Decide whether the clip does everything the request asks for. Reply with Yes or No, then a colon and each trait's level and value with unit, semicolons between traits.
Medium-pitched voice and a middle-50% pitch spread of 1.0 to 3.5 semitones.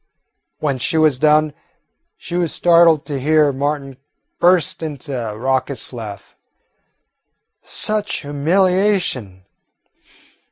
No: medium, 150 Hz; average, 4.3 semitones